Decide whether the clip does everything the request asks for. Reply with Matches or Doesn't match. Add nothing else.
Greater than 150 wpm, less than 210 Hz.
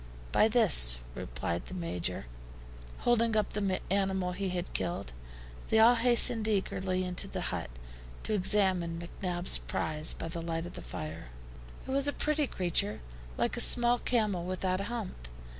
Matches